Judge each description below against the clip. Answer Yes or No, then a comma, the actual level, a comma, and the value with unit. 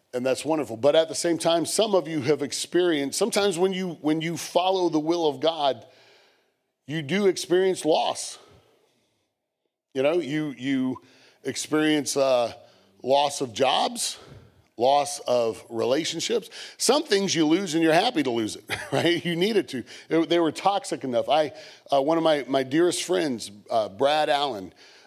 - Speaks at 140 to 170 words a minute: Yes, average, 165 wpm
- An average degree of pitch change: Yes, average, 3.8 semitones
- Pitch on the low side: No, medium, 160 Hz